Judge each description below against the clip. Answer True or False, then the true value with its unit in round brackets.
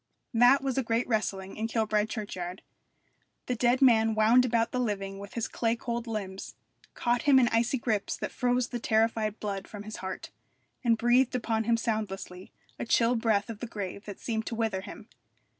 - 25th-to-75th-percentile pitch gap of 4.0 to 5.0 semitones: False (2.5 semitones)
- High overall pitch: True (225 Hz)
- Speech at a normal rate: True (190 wpm)